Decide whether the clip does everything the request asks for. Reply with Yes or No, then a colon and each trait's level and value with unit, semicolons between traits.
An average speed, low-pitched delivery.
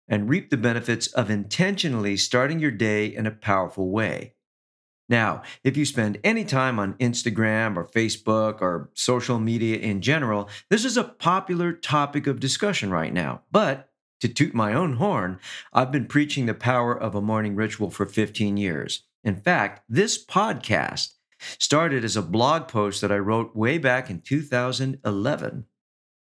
Yes: average, 160 wpm; low, 110 Hz